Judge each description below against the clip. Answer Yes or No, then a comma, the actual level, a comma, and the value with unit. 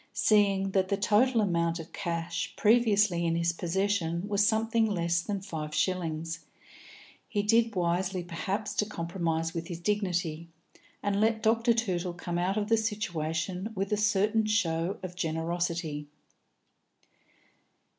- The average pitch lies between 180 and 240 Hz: Yes, medium, 185 Hz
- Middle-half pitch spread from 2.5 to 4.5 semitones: Yes, average, 3.7 semitones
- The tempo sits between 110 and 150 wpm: Yes, slow, 135 wpm